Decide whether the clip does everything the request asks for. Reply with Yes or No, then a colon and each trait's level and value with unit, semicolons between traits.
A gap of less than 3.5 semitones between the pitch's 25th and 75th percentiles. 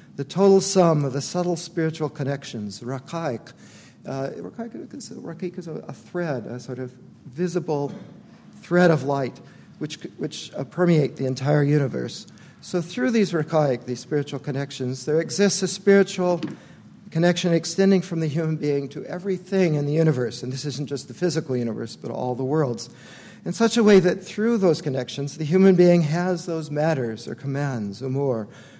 No: average, 4.7 semitones